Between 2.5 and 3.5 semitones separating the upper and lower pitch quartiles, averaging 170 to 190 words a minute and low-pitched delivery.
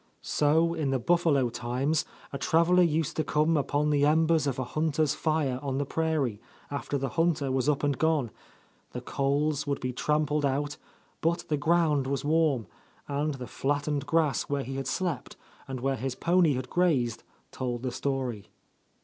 No: average, 2.9 semitones; average, 175 wpm; medium, 145 Hz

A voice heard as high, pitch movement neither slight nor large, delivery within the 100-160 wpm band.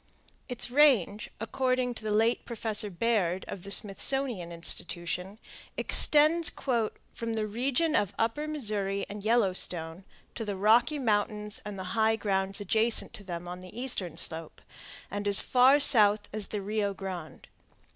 Yes: high, 210 Hz; average, 3.6 semitones; average, 150 wpm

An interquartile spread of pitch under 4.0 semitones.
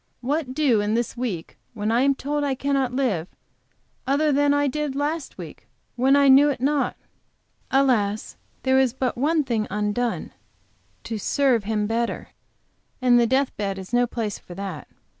No: average, 4.3 semitones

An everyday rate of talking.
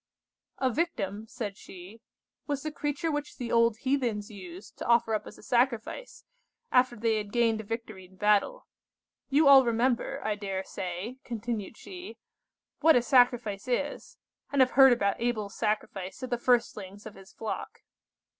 Yes: average, 165 wpm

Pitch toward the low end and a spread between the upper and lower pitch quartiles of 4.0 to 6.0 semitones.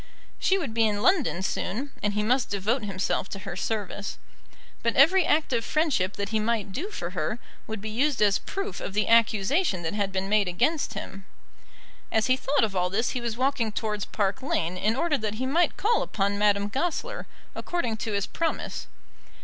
No: high, 220 Hz; average, 5.2 semitones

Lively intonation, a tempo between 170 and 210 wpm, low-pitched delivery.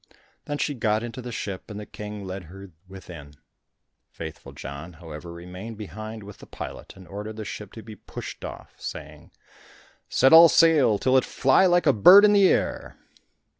Yes: wide, 5.8 semitones; average, 175 wpm; low, 105 Hz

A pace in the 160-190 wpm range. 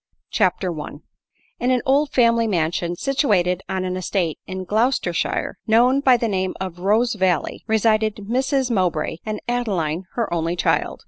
No: average, 145 wpm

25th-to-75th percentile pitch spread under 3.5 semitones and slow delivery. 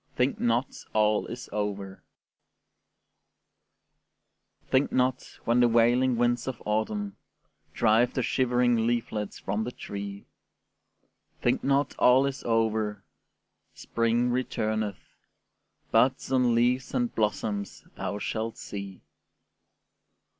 Yes: average, 2.8 semitones; slow, 105 wpm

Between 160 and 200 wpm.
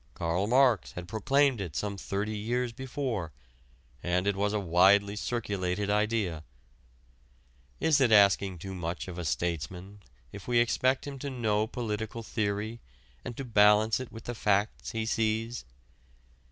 No: average, 150 wpm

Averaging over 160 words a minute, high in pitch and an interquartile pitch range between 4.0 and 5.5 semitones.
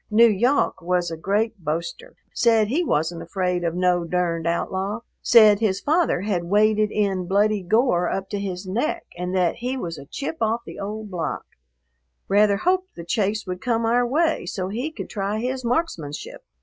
Yes: average, 175 wpm; high, 205 Hz; average, 4.6 semitones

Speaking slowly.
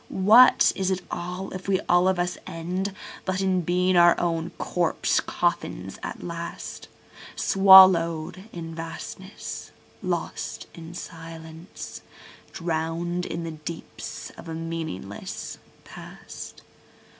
Yes: slow, 110 wpm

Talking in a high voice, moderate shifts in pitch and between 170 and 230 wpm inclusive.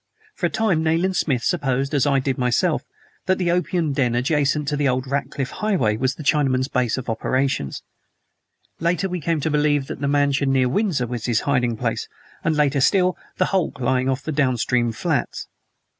No: medium, 140 Hz; average, 3.6 semitones; average, 190 wpm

